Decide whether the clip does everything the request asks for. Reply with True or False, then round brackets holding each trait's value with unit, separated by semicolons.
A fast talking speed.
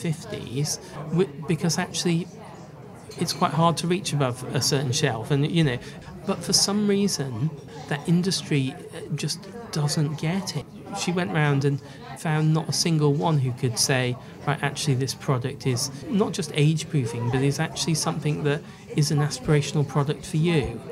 False (165 wpm)